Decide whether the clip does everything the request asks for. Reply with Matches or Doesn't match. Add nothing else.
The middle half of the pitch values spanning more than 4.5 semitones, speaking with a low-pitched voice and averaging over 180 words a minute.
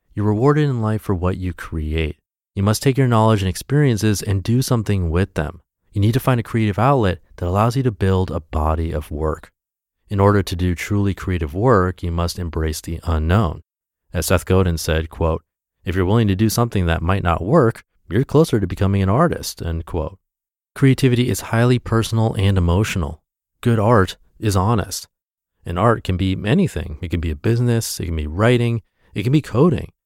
Matches